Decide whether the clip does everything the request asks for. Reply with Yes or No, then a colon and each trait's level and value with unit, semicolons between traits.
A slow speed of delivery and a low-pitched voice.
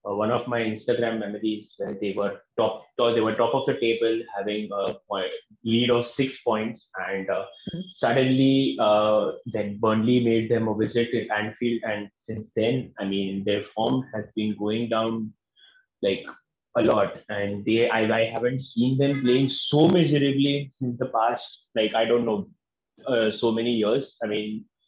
No: average, 170 wpm; low, 115 Hz